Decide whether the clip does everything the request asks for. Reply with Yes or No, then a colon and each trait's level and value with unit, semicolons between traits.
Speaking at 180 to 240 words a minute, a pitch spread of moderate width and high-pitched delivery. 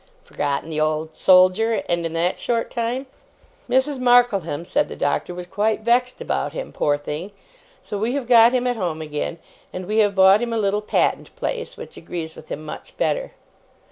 No: average, 190 wpm; wide, 6.5 semitones; high, 205 Hz